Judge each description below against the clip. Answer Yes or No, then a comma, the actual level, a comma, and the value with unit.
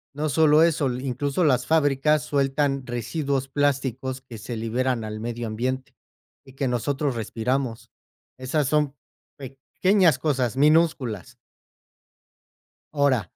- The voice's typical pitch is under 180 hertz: Yes, low, 135 Hz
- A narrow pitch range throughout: No, average, 3.1 semitones